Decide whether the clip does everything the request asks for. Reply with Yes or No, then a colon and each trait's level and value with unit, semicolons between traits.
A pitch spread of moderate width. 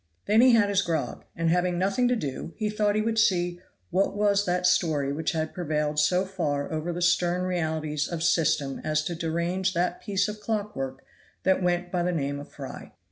Yes: average, 3.8 semitones